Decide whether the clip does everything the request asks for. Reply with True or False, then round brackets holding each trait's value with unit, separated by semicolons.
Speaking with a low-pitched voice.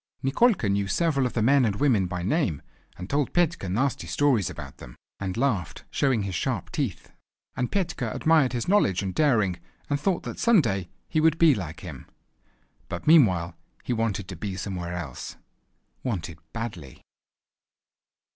True (115 Hz)